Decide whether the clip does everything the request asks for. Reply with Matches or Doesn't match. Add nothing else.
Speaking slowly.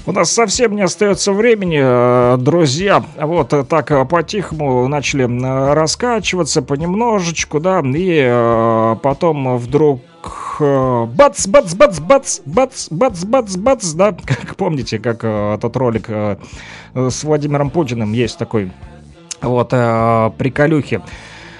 Matches